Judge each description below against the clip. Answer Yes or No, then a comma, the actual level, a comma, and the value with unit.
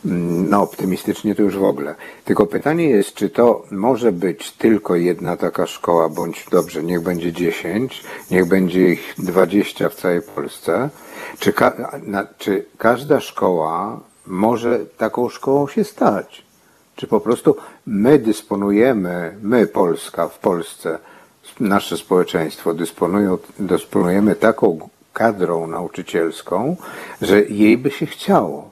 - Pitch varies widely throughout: No, average, 3.2 semitones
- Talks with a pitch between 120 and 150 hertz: No, very low, 95 Hz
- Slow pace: No, average, 125 wpm